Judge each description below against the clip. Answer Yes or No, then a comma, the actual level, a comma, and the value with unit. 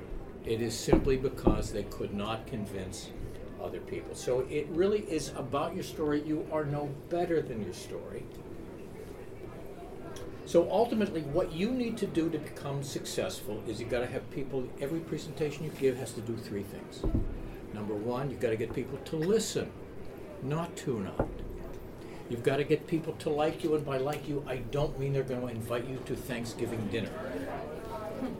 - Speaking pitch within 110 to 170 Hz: Yes, medium, 140 Hz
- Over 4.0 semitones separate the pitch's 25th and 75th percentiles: Yes, average, 4.6 semitones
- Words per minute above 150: Yes, average, 180 wpm